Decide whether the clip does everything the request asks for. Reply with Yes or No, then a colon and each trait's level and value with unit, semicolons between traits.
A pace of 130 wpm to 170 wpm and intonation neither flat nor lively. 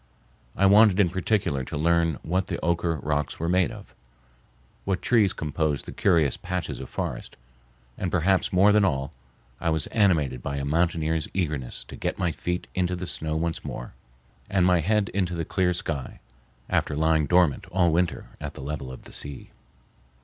No: average, 180 wpm; average, 3.4 semitones